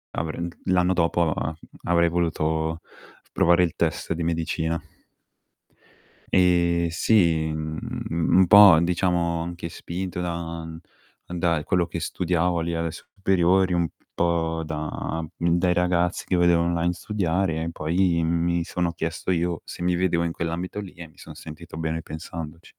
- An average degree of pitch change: No, narrow, 1.3 semitones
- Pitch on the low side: Yes, very low, 85 Hz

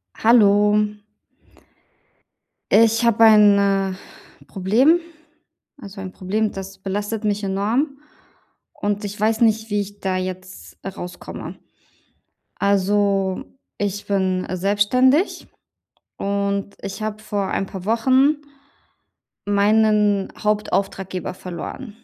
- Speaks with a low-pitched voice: No, high, 205 Hz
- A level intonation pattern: Yes, narrow, 1.9 semitones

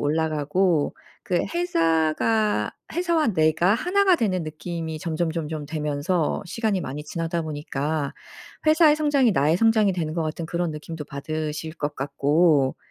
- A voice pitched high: No, medium, 160 Hz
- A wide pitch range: No, average, 4.4 semitones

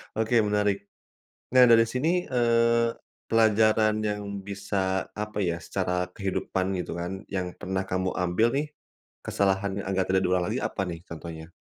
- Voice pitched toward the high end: No, low, 100 Hz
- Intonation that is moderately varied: Yes, average, 3.3 semitones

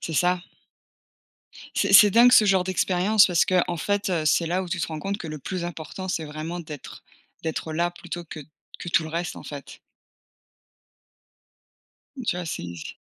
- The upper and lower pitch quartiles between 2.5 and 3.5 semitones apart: Yes, average, 2.9 semitones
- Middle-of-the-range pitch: Yes, medium, 175 Hz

